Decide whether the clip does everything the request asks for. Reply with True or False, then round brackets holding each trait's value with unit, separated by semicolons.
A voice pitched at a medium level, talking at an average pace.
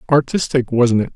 False (130 Hz; 155 wpm)